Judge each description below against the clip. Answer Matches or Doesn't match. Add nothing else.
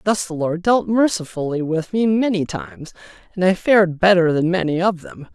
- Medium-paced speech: Matches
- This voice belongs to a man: Matches